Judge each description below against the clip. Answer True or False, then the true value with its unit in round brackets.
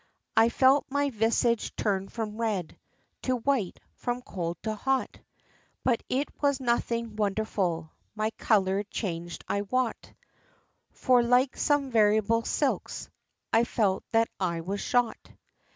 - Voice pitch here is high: True (225 Hz)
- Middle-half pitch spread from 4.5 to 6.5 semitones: False (3.7 semitones)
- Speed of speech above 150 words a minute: False (135 wpm)